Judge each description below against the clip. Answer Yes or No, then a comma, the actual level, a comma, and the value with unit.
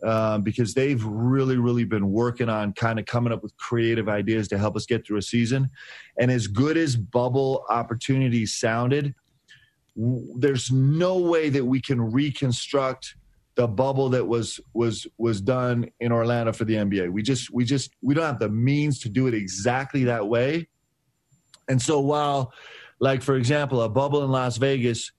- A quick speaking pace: No, average, 185 wpm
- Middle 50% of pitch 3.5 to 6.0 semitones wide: No, average, 2.9 semitones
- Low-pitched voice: Yes, low, 125 Hz